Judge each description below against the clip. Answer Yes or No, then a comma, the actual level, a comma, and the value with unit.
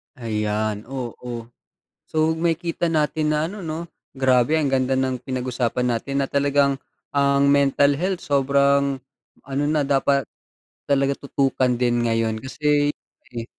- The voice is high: No, medium, 140 Hz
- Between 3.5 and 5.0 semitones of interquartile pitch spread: No, narrow, 2.6 semitones